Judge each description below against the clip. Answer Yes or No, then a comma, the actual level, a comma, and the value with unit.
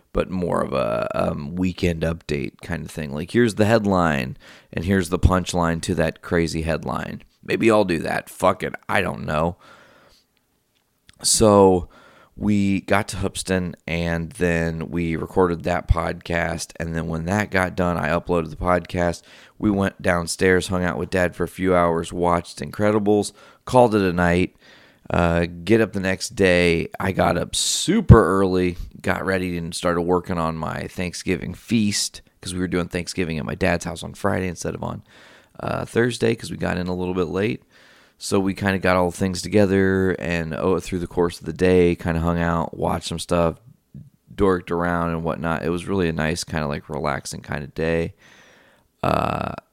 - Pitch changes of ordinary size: No, narrow, 2.2 semitones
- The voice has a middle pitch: No, very low, 90 Hz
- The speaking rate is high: No, average, 185 wpm